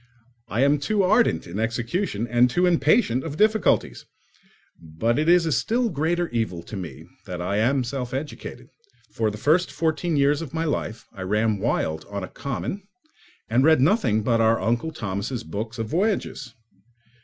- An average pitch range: No, wide, 6.8 semitones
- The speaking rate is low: No, average, 170 wpm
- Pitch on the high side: No, low, 125 Hz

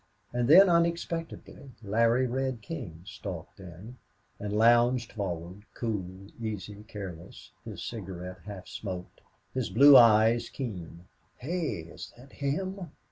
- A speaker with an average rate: No, slow, 120 wpm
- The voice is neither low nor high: No, low, 110 Hz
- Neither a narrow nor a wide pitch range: No, wide, 5.7 semitones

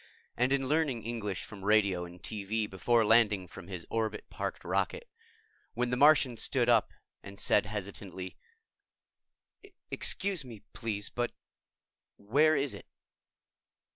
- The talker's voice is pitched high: No, low, 110 Hz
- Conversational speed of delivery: No, slow, 130 wpm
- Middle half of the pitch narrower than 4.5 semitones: Yes, average, 4.0 semitones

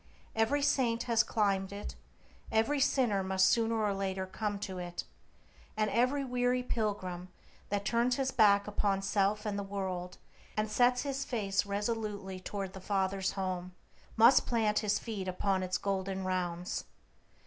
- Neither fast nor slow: Yes, average, 150 wpm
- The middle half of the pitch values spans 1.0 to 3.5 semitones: Yes, average, 3.2 semitones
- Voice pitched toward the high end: Yes, high, 205 Hz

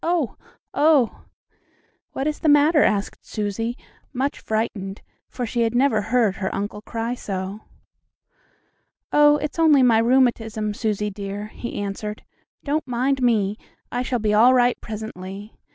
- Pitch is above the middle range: Yes, high, 230 Hz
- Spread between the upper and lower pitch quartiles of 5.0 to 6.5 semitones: No, average, 3.9 semitones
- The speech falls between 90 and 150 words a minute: Yes, average, 140 wpm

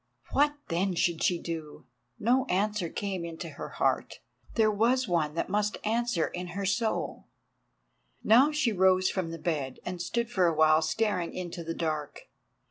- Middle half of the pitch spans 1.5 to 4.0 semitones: No, average, 4.6 semitones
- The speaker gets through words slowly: No, average, 160 wpm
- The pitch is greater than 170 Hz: Yes, medium, 185 Hz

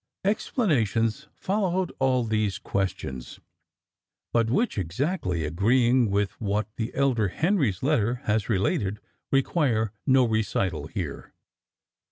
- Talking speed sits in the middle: No, slow, 105 wpm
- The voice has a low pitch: Yes, low, 115 Hz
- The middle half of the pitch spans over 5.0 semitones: Yes, wide, 5.5 semitones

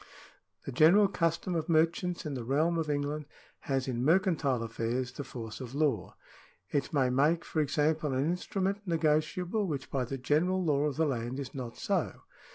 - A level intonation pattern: No, average, 4.0 semitones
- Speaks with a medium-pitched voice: Yes, medium, 150 Hz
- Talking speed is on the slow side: No, average, 175 wpm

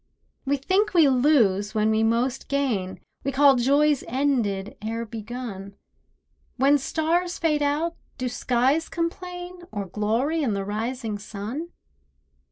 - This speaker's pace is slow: Yes, slow, 130 wpm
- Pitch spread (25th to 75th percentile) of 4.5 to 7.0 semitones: Yes, wide, 5.5 semitones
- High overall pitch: Yes, very high, 255 Hz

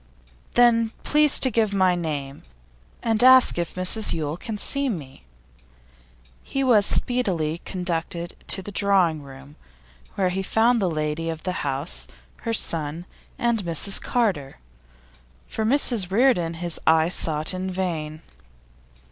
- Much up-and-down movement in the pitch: Yes, wide, 5.8 semitones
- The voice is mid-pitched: Yes, medium, 180 Hz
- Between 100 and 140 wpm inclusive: Yes, slow, 135 wpm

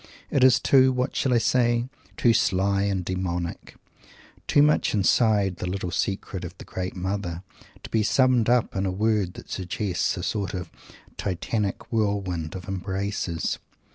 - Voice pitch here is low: Yes, low, 100 Hz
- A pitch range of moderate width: Yes, average, 3.7 semitones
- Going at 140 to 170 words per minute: Yes, average, 160 wpm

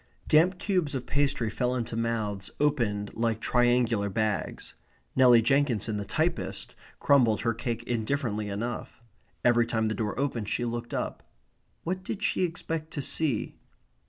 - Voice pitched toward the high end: No, low, 120 Hz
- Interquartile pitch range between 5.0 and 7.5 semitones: No, average, 4.3 semitones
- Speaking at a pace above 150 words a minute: No, average, 145 wpm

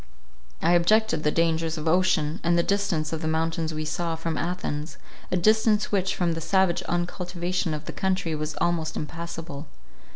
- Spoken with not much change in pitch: Yes, narrow, 2.3 semitones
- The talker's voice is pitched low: No, medium, 170 Hz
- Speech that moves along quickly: No, average, 170 wpm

